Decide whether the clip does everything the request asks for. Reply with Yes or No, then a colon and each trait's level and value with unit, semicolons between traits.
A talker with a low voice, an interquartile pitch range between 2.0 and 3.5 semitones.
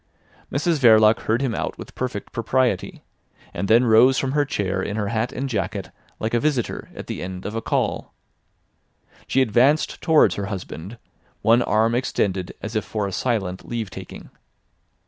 No: low, 115 Hz; average, 4.0 semitones